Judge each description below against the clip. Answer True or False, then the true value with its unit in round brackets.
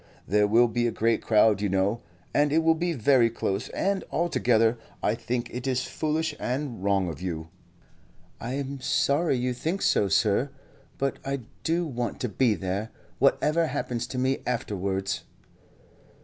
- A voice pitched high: False (120 Hz)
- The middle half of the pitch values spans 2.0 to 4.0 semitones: False (5.1 semitones)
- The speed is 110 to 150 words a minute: False (165 wpm)